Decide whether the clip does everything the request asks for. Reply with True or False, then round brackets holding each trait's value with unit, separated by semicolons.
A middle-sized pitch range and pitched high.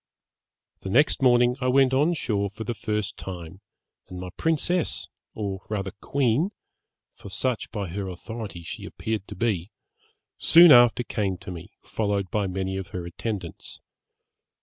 False (4.3 semitones; 105 Hz)